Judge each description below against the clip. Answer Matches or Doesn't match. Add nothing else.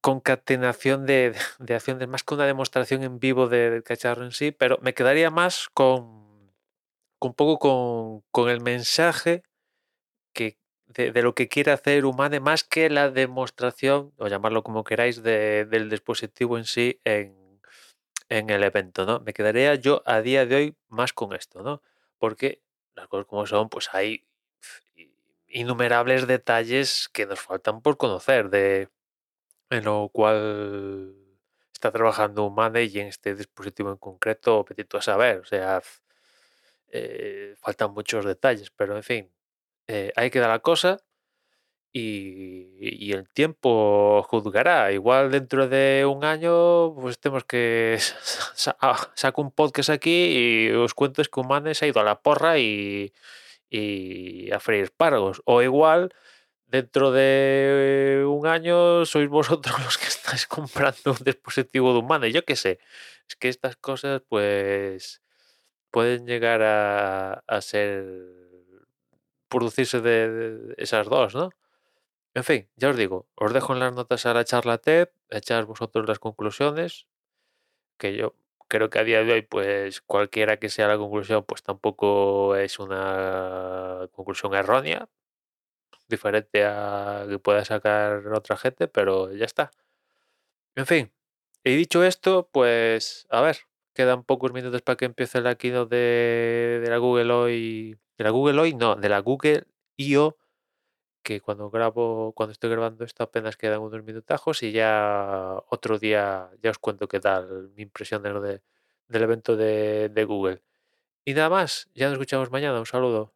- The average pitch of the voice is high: Doesn't match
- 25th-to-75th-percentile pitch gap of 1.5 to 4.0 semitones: Doesn't match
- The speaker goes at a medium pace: Matches